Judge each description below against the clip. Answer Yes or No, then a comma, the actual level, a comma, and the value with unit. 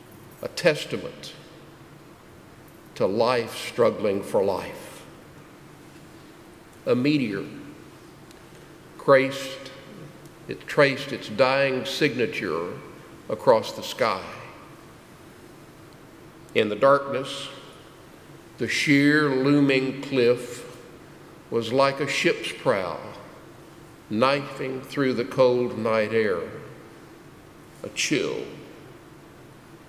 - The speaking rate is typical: No, slow, 75 wpm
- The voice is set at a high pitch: No, medium, 140 Hz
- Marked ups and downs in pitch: No, average, 2.7 semitones